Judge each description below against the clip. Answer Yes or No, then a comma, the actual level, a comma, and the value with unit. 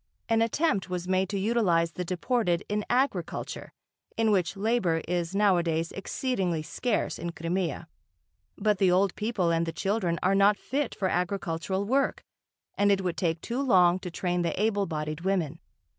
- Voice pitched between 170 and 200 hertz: Yes, high, 190 Hz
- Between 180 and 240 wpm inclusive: No, average, 165 wpm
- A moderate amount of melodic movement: Yes, average, 3.6 semitones